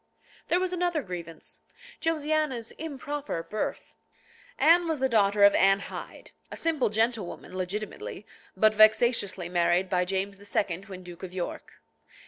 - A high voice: Yes, high, 210 Hz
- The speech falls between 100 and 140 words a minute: Yes, slow, 135 wpm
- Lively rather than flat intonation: Yes, wide, 7.7 semitones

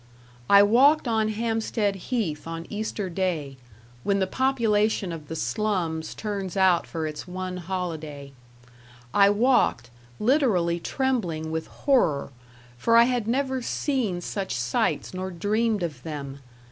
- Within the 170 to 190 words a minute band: No, slow, 135 wpm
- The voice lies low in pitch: No, high, 190 Hz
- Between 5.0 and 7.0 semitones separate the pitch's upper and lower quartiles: Yes, wide, 5.5 semitones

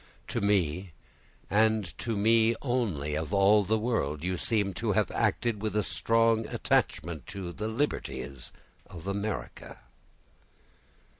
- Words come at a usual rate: No, slow, 130 wpm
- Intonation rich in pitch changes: No, average, 4.4 semitones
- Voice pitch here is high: No, low, 100 Hz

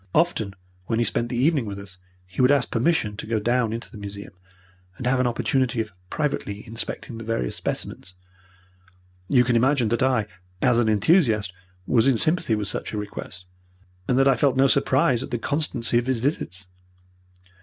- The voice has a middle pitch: No, low, 120 Hz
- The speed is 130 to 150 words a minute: No, average, 185 wpm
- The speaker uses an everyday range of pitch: Yes, average, 3.8 semitones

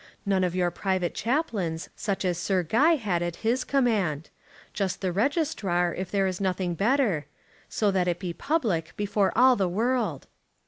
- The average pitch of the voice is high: Yes, high, 195 Hz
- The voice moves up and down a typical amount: Yes, average, 4.5 semitones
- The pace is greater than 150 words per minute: Yes, average, 170 wpm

